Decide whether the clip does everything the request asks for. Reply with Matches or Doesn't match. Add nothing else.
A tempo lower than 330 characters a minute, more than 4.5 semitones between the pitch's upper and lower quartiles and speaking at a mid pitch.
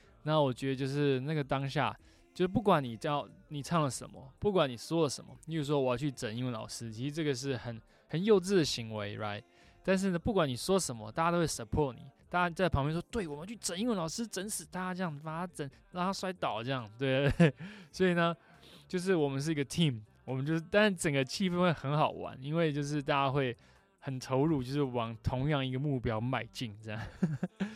Doesn't match